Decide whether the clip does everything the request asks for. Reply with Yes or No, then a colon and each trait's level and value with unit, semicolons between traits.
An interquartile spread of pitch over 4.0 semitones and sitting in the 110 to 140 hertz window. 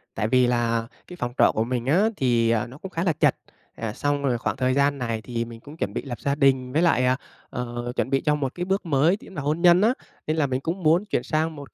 Yes: average, 4.7 semitones; low, 135 Hz